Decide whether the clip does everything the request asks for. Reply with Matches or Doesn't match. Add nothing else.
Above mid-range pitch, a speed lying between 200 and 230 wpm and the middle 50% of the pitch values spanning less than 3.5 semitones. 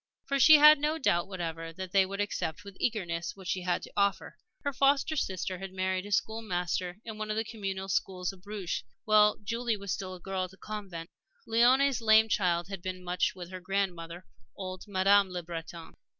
Matches